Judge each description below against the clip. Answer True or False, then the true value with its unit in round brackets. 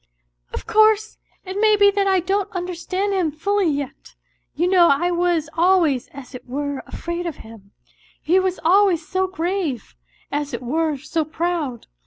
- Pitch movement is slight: False (4.6 semitones)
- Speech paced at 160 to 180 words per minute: True (170 wpm)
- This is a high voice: True (345 Hz)